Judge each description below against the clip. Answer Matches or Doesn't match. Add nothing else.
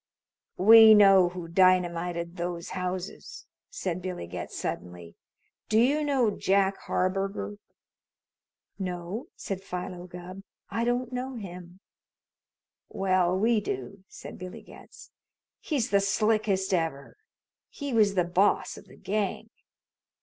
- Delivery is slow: Matches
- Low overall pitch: Doesn't match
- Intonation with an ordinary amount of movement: Matches